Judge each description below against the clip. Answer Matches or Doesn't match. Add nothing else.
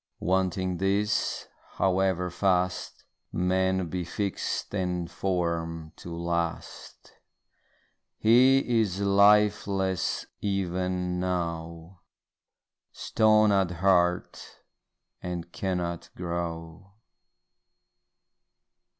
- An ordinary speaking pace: Doesn't match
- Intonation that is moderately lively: Doesn't match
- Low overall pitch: Matches